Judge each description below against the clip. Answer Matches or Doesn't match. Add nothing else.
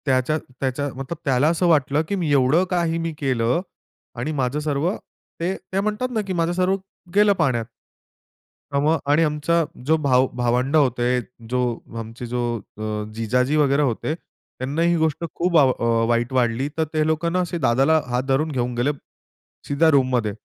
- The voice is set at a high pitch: Doesn't match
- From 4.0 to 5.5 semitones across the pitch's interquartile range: Matches